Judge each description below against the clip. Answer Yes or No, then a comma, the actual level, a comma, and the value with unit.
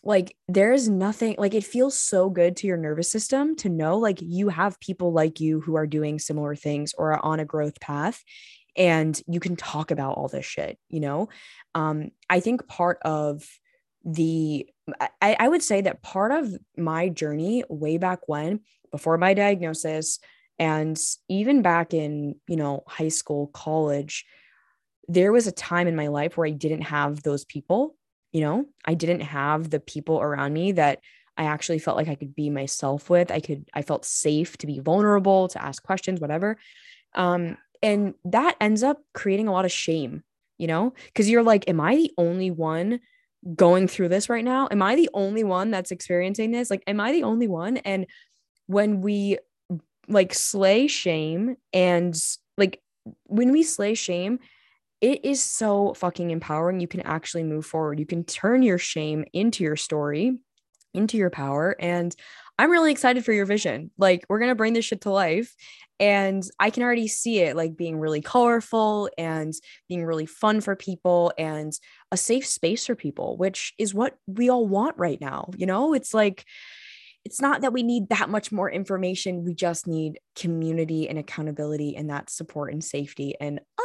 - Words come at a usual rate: Yes, average, 185 wpm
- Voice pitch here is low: No, medium, 180 Hz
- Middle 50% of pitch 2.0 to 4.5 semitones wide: No, average, 5.3 semitones